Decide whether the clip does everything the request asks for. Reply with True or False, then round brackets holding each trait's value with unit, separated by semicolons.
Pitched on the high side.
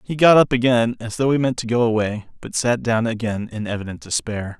False (115 Hz)